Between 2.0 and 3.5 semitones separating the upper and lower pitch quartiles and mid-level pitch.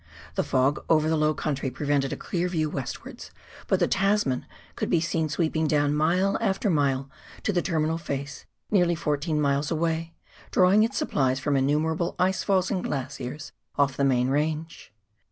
Yes: average, 3.2 semitones; medium, 155 Hz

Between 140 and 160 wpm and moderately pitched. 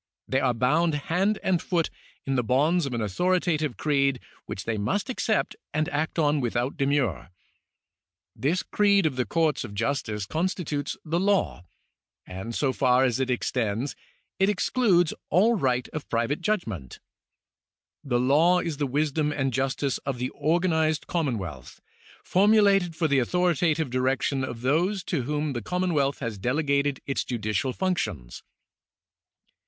Yes: average, 150 wpm; medium, 145 Hz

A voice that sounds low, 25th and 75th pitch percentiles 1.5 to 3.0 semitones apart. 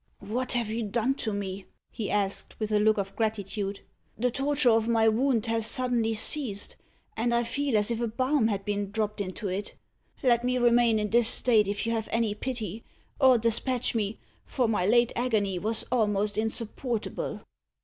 No: high, 225 Hz; narrow, 2.5 semitones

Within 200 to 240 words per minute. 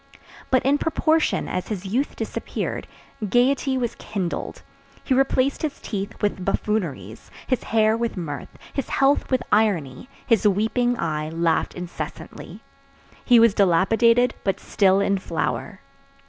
No: slow, 135 wpm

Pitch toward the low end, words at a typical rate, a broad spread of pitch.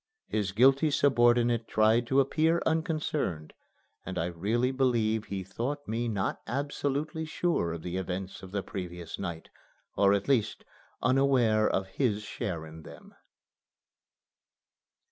No: low, 110 Hz; slow, 130 wpm; wide, 6.1 semitones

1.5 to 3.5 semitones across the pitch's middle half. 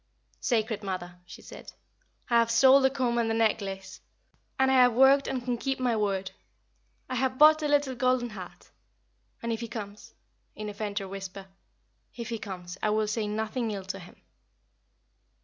No: average, 4.1 semitones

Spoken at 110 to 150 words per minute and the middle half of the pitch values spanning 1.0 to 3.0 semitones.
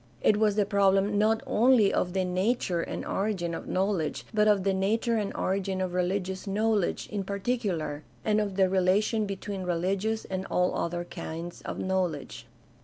No: average, 175 wpm; narrow, 2.4 semitones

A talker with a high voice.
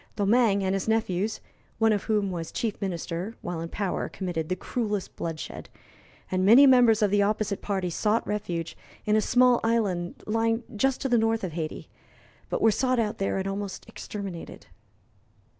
Yes: high, 205 Hz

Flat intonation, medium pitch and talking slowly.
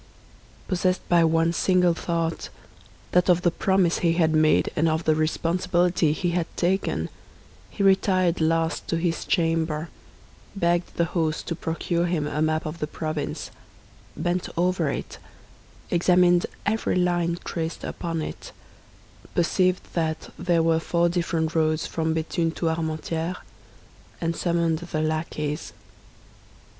Yes: narrow, 1.6 semitones; medium, 170 Hz; slow, 130 wpm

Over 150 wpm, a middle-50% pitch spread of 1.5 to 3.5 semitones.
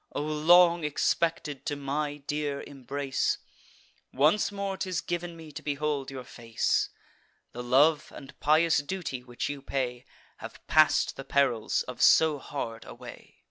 No: average, 145 wpm; average, 2.9 semitones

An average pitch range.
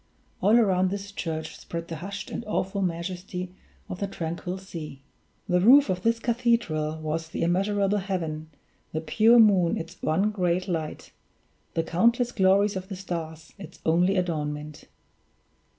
Yes: average, 3.5 semitones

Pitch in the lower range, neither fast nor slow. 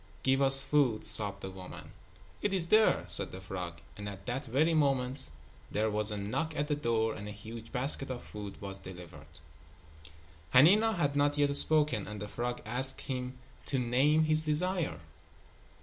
Yes: low, 125 Hz; average, 175 wpm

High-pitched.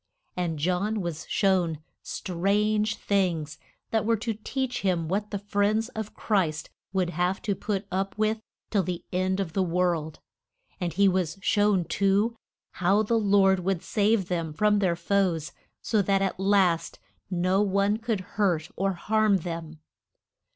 Yes: high, 195 Hz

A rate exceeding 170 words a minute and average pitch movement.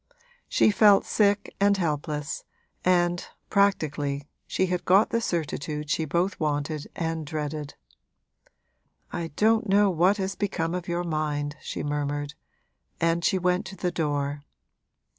No: slow, 135 wpm; average, 4.3 semitones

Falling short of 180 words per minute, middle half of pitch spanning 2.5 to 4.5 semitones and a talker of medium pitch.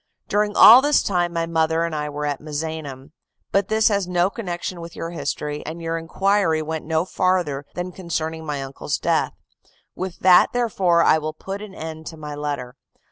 No: average, 190 wpm; average, 3.2 semitones; medium, 165 Hz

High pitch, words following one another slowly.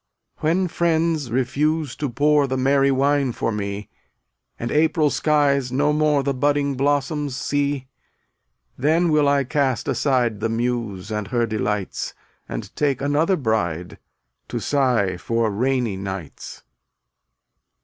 No: low, 135 Hz; slow, 130 wpm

